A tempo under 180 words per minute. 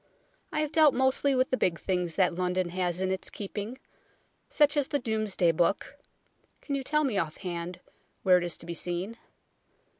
No: average, 185 wpm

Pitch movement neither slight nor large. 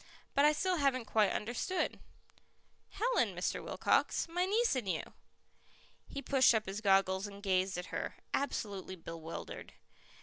No: wide, 7.2 semitones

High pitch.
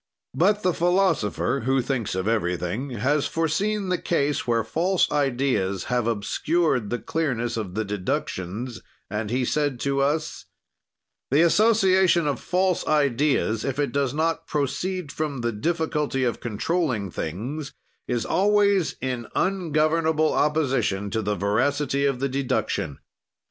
No: medium, 140 Hz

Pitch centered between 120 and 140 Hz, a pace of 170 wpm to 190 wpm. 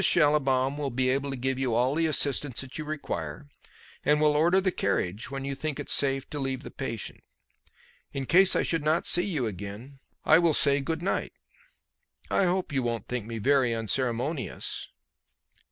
Yes: low, 135 Hz; average, 185 wpm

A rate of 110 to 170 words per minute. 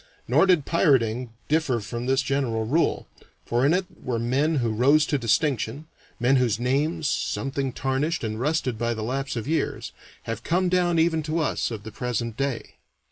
No: average, 180 wpm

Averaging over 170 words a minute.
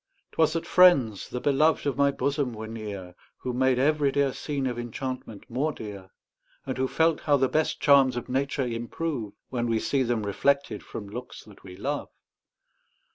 Yes: average, 180 wpm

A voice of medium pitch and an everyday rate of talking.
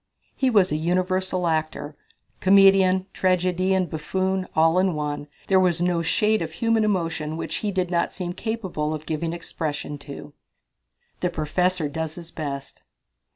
Yes: medium, 175 Hz; average, 150 wpm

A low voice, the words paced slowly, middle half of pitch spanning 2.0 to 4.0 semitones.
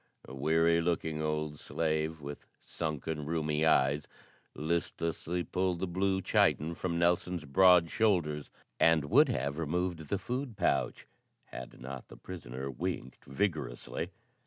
Yes: very low, 80 Hz; slow, 130 wpm; average, 3.0 semitones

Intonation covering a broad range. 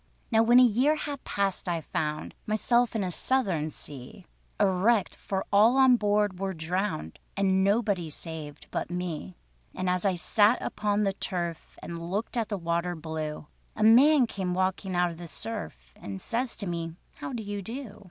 No: average, 4.5 semitones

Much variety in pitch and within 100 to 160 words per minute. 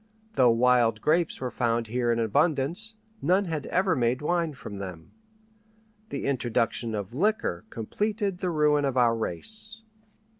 Yes: wide, 7.2 semitones; average, 145 wpm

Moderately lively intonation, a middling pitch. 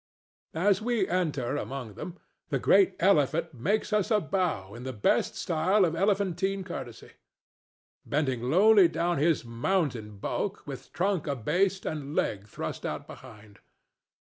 No: wide, 7.1 semitones; medium, 165 Hz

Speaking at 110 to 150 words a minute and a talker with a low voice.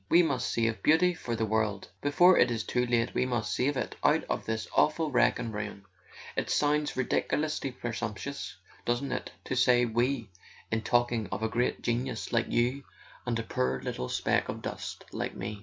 No: average, 190 wpm; low, 120 Hz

